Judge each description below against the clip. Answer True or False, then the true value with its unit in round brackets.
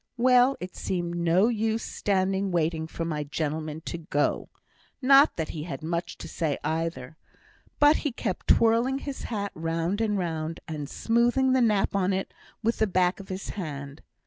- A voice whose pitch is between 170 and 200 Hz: True (185 Hz)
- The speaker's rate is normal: True (170 wpm)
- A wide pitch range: True (5.8 semitones)